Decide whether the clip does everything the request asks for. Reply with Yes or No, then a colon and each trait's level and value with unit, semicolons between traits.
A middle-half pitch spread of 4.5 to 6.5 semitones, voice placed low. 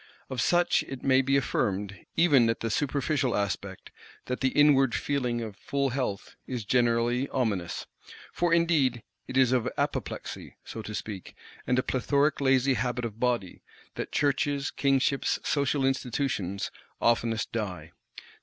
No: average, 3.3 semitones; low, 125 Hz